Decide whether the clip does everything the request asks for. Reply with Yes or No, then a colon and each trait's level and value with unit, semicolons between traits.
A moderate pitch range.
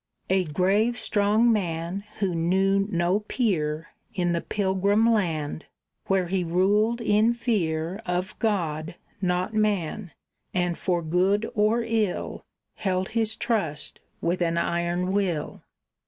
Yes: average, 3.6 semitones